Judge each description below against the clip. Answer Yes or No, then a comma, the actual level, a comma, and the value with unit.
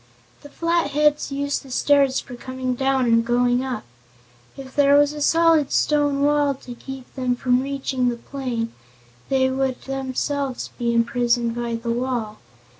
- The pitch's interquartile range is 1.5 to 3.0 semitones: Yes, narrow, 2.5 semitones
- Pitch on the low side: No, very high, 260 Hz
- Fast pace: No, average, 155 wpm